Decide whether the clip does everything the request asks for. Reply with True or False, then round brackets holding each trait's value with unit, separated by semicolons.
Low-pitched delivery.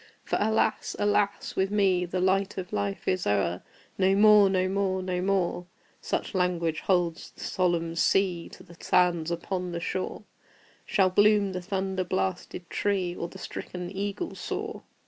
False (185 Hz)